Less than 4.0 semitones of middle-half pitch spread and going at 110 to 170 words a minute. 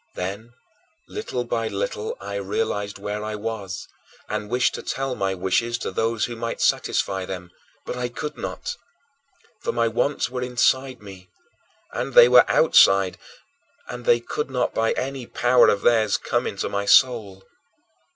Yes: average, 3.6 semitones; average, 160 wpm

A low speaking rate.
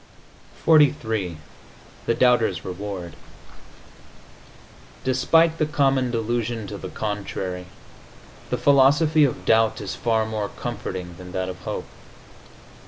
Yes: slow, 105 wpm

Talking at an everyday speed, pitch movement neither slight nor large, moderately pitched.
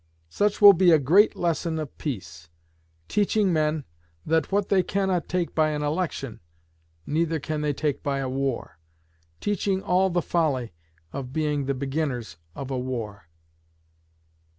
Yes: average, 150 wpm; average, 4.8 semitones; medium, 155 Hz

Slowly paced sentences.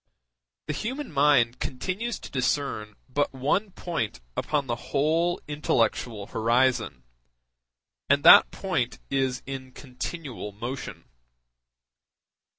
Yes: slow, 100 wpm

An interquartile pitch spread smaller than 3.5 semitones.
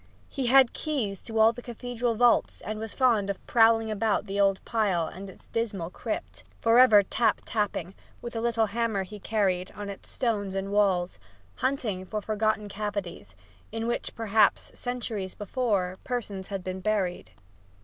Yes: average, 2.9 semitones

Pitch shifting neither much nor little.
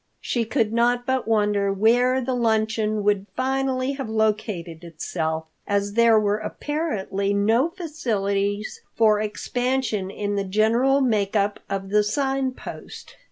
Yes: average, 3.9 semitones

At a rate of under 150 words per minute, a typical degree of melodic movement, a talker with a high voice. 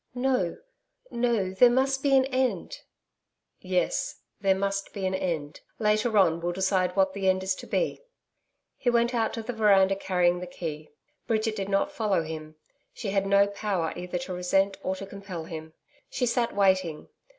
No: average, 175 wpm; average, 3.7 semitones; high, 195 Hz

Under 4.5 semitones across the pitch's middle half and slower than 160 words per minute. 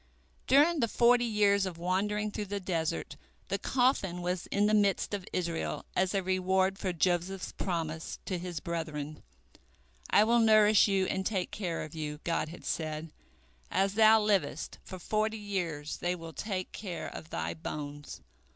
No: average, 3.8 semitones; average, 165 wpm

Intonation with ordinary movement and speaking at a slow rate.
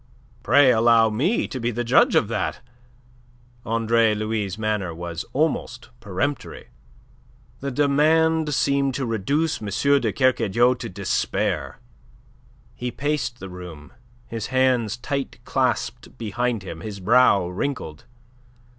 Yes: average, 4.4 semitones; slow, 120 wpm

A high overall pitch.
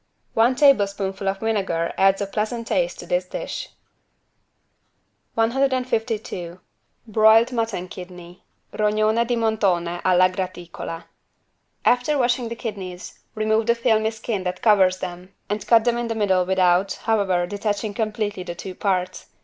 Yes: high, 210 Hz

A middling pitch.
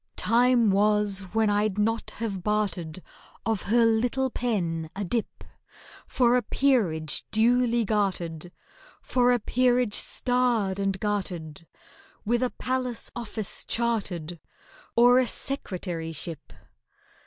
No: high, 215 Hz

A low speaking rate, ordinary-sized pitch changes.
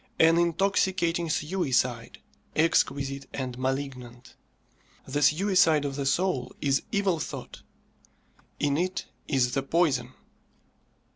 Yes: slow, 100 wpm; average, 4.4 semitones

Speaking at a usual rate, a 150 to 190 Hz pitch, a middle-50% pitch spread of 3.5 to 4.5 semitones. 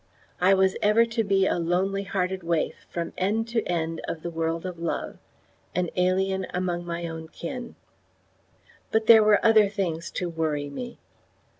No: average, 165 wpm; medium, 185 Hz; average, 3.1 semitones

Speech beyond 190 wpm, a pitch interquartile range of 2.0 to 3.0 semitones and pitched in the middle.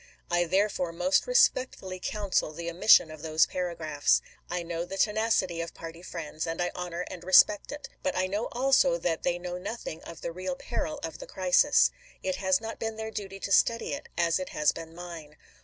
No: fast, 205 wpm; average, 4.7 semitones; medium, 180 Hz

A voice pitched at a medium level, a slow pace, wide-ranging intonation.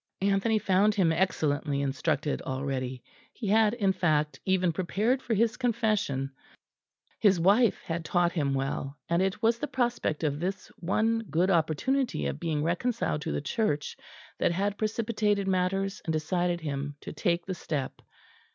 No: medium, 180 Hz; average, 155 wpm; wide, 5.8 semitones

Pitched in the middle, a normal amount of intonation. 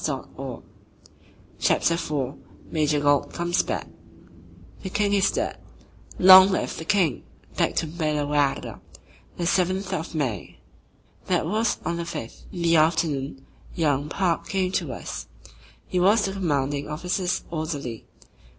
Yes: medium, 165 Hz; average, 4.2 semitones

